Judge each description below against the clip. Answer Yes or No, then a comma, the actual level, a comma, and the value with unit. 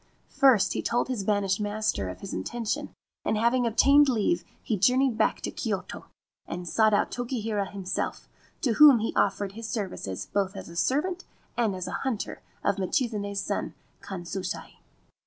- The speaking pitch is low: No, high, 215 Hz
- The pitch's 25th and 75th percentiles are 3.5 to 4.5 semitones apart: Yes, average, 4.0 semitones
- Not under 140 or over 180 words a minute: Yes, average, 160 wpm